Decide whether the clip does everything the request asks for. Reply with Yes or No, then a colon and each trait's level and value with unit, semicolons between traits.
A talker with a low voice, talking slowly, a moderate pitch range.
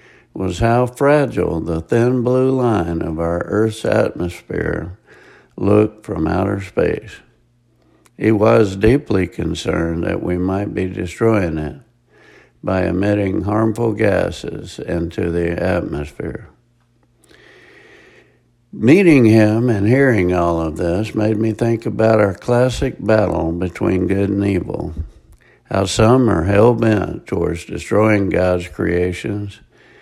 Yes: low, 105 Hz; slow, 120 wpm; average, 4.7 semitones